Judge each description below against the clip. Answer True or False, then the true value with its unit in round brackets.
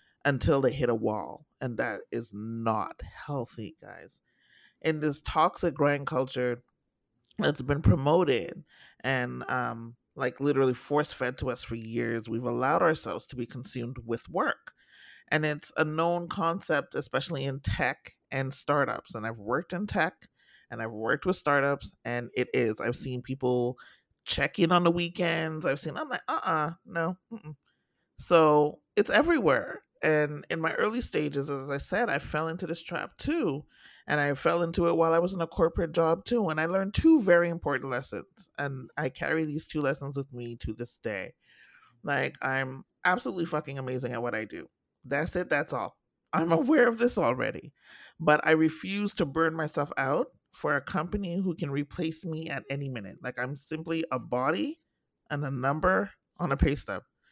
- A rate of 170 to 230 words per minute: True (175 wpm)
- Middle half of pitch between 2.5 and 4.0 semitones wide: False (4.9 semitones)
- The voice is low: False (150 Hz)